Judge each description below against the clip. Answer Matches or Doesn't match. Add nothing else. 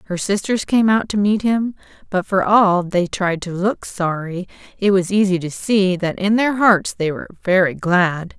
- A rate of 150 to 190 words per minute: Doesn't match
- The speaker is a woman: Matches